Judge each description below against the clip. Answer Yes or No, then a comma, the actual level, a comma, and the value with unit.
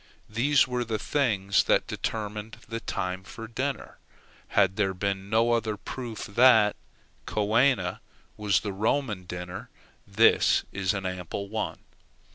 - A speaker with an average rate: No, slow, 130 wpm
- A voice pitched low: Yes, low, 105 Hz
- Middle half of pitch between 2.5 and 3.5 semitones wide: Yes, average, 3.0 semitones